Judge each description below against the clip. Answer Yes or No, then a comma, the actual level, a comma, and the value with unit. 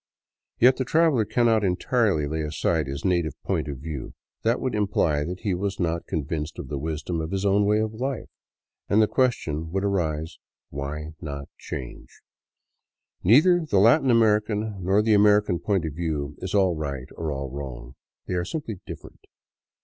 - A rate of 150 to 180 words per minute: Yes, average, 170 wpm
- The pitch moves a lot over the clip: Yes, wide, 5.9 semitones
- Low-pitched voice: Yes, very low, 90 Hz